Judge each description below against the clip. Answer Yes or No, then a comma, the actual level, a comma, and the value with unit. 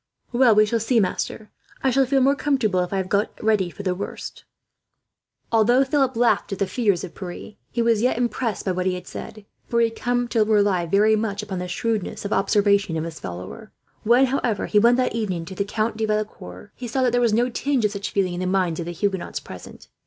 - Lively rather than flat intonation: No, average, 3.9 semitones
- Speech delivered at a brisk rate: Yes, fast, 235 wpm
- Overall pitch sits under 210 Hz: No, high, 215 Hz